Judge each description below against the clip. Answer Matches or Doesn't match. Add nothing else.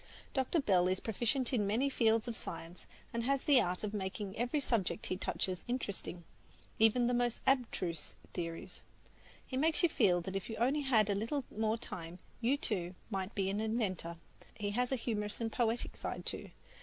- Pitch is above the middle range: Matches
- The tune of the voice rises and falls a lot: Doesn't match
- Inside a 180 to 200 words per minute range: Matches